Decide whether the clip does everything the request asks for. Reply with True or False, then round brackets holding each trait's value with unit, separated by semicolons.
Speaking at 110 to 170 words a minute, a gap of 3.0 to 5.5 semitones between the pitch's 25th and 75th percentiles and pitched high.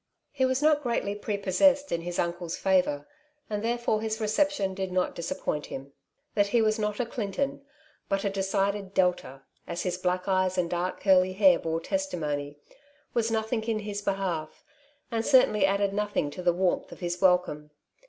False (180 wpm; 3.6 semitones; 195 Hz)